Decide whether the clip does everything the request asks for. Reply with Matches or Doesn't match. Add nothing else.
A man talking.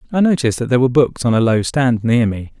Matches